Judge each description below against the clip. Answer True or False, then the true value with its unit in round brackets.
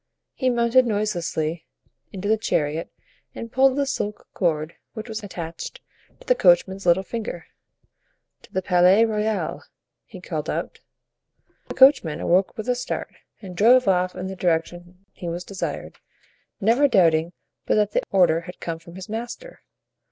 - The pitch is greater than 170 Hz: True (190 Hz)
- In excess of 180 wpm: False (155 wpm)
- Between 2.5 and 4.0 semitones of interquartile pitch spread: False (4.7 semitones)